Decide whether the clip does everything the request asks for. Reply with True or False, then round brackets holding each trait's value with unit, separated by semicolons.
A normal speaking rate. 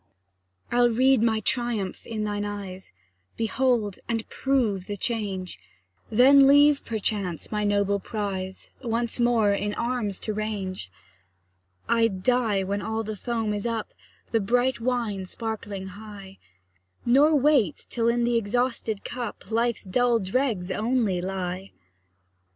False (130 wpm)